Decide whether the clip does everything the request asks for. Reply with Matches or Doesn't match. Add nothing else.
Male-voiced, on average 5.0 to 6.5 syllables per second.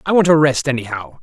Matches